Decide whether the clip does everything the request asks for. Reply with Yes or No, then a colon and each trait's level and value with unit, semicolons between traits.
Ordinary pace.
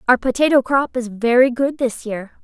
Yes: average, 195 wpm